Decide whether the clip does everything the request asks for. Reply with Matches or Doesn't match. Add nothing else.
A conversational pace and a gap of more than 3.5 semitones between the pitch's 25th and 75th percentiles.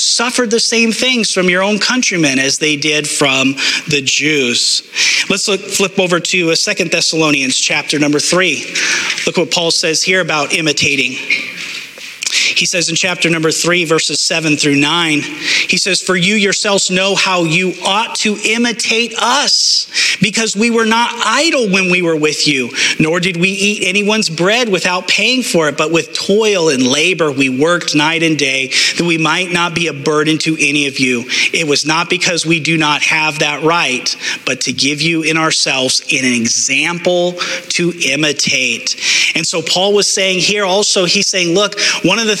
Matches